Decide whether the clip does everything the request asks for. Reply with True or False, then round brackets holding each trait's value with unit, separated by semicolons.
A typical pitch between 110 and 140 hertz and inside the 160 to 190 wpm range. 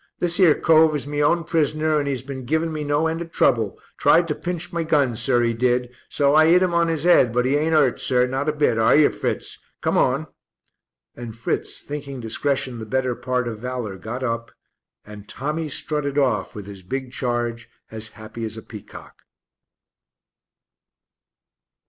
True (135 Hz; 185 wpm)